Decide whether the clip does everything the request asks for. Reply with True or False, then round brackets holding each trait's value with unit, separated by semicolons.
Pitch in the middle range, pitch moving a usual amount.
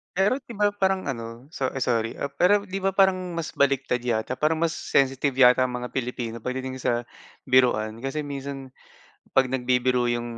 False (130 Hz; 4.2 semitones)